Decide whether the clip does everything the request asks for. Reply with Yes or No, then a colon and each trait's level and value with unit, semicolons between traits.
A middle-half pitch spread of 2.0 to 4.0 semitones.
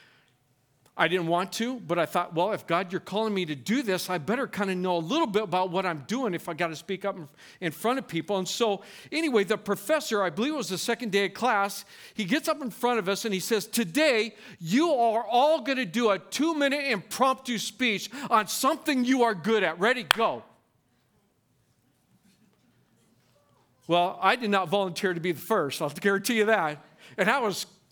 No: average, 5.0 semitones